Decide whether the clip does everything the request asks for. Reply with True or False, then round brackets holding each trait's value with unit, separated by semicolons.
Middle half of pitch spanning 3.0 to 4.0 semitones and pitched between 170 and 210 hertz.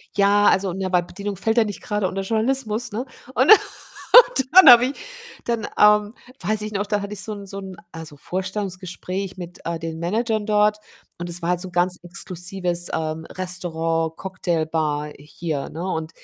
True (3.5 semitones; 190 Hz)